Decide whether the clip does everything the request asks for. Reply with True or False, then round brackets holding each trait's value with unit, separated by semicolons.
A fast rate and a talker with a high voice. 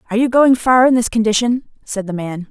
True (240 wpm; 230 Hz)